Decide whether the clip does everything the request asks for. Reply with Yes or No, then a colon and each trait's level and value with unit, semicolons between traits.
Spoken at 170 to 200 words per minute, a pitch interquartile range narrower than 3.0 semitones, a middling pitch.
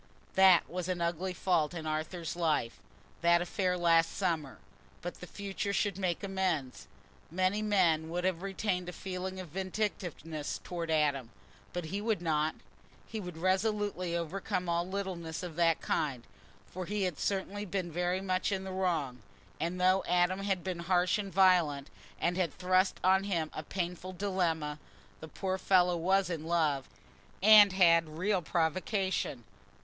No: average, 155 wpm; narrow, 2.4 semitones; medium, 180 Hz